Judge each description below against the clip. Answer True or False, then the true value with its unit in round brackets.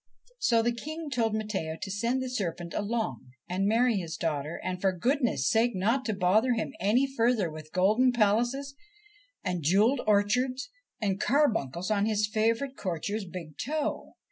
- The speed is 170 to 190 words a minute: False (160 wpm)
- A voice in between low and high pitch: False (215 Hz)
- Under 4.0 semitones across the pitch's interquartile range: False (4.9 semitones)